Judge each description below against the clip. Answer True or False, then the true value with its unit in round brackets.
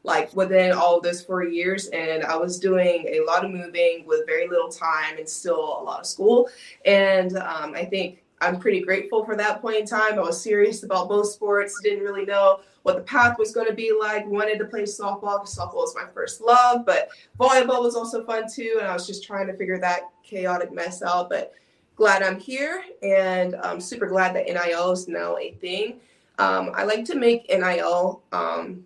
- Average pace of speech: False (215 wpm)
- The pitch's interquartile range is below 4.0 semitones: False (4.3 semitones)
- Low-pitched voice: False (200 Hz)